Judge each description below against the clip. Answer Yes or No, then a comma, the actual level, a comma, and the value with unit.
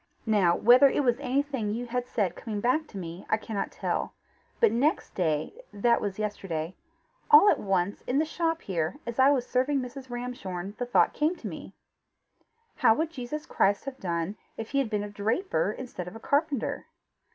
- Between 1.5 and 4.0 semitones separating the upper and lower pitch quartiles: No, wide, 5.4 semitones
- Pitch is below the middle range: No, high, 240 Hz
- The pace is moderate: Yes, average, 190 wpm